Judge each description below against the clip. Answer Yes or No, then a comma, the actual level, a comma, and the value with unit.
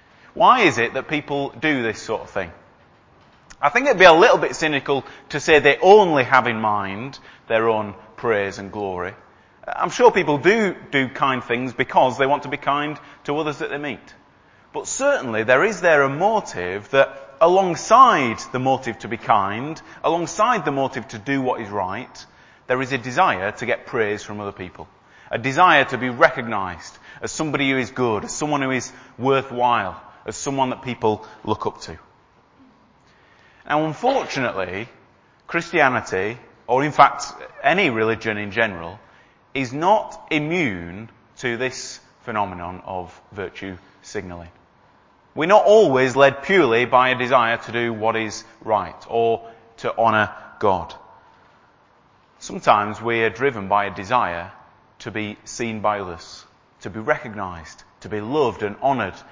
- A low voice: Yes, low, 120 Hz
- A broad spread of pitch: No, average, 4.7 semitones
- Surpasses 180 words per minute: No, average, 160 wpm